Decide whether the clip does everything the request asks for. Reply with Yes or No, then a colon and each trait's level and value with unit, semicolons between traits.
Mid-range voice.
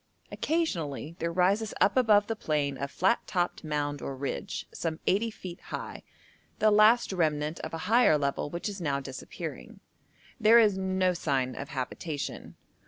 Yes: medium, 175 Hz